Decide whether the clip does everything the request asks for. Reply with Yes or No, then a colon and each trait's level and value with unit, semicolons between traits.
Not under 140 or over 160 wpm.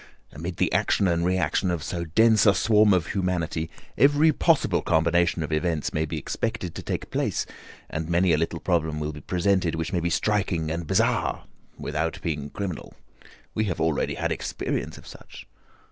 No: average, 175 wpm